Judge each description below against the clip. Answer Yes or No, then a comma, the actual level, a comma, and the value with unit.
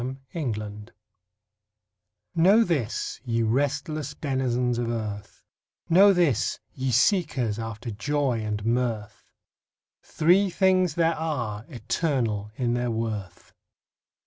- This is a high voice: No, low, 125 Hz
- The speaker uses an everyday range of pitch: No, wide, 5.7 semitones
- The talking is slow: Yes, slow, 105 wpm